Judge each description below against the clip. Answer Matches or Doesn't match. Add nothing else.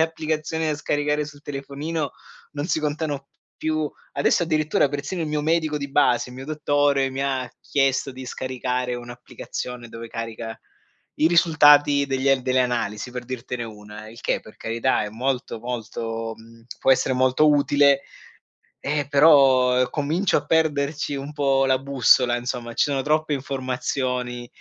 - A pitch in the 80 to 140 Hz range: Matches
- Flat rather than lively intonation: Doesn't match